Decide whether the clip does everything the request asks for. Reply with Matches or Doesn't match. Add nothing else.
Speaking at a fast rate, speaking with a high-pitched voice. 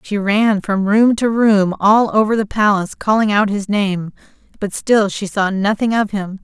Doesn't match